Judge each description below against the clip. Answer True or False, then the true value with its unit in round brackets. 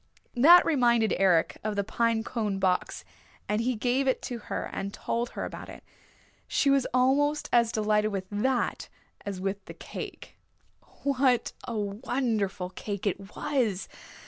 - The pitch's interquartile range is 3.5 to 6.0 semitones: True (4.0 semitones)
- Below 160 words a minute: True (150 wpm)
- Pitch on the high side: True (225 Hz)